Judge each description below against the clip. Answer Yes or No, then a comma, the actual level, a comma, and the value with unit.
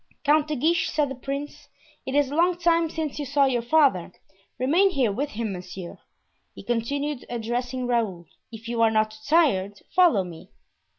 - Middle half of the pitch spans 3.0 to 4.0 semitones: No, average, 5.1 semitones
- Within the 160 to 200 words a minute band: Yes, average, 180 wpm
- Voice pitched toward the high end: Yes, very high, 260 Hz